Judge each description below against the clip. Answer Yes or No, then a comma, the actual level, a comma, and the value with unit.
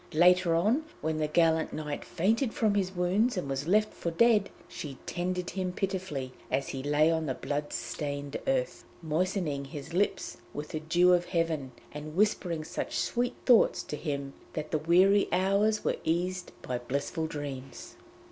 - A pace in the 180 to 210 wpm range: No, average, 165 wpm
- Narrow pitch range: No, average, 4.2 semitones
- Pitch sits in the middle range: Yes, medium, 165 Hz